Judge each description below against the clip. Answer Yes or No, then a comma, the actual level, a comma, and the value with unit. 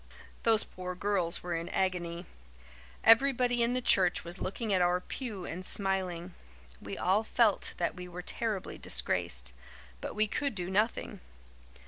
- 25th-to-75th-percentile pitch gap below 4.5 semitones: Yes, average, 3.9 semitones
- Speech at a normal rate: Yes, average, 155 wpm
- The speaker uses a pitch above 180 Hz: Yes, high, 190 Hz